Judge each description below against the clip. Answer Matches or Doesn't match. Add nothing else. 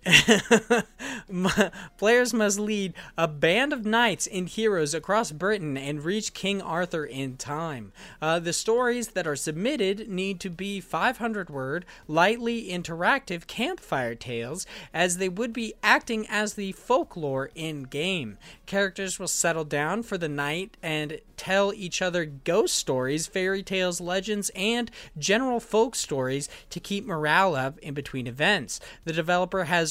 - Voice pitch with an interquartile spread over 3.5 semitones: Matches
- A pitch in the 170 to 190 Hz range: Matches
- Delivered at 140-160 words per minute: Matches